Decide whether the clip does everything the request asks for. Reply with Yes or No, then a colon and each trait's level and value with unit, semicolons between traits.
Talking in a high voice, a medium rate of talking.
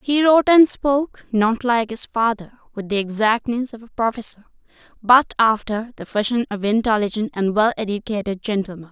Yes: high, 225 Hz; average, 160 wpm